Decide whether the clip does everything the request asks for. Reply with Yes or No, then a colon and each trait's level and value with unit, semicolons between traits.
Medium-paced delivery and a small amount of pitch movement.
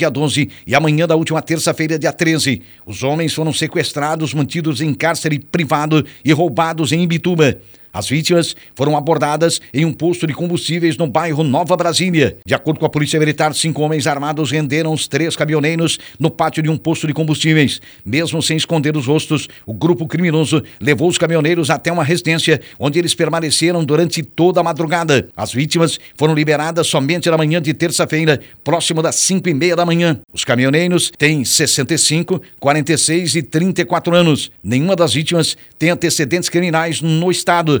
Yes: average, 170 wpm; narrow, 1.9 semitones